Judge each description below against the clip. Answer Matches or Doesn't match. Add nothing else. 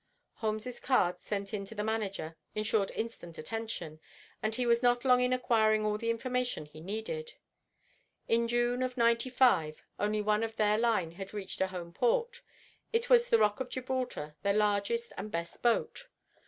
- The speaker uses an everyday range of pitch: Matches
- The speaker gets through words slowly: Doesn't match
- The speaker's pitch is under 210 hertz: Doesn't match